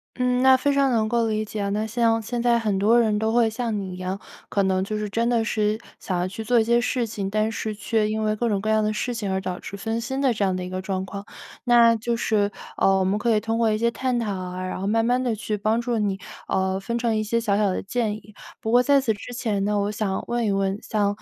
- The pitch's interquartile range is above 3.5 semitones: No, average, 2.7 semitones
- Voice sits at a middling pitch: No, high, 215 Hz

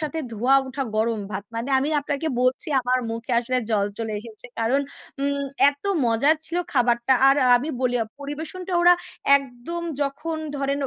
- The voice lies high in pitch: Yes, very high, 265 Hz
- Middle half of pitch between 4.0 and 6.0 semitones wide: No, average, 3.4 semitones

